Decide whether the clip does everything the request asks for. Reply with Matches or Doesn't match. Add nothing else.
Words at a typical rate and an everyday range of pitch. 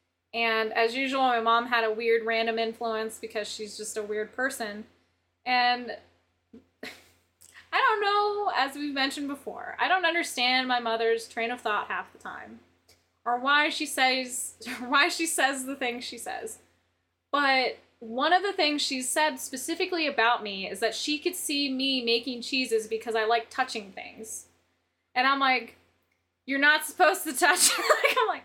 Matches